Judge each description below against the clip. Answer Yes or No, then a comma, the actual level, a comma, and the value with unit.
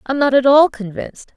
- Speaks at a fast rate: Yes, fast, 220 wpm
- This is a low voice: No, very high, 260 Hz